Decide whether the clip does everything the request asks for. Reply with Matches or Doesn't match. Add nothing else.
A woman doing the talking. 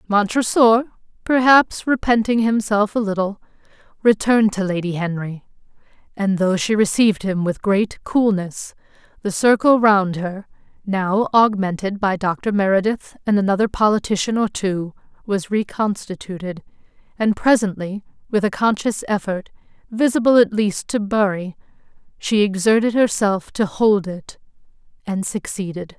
Matches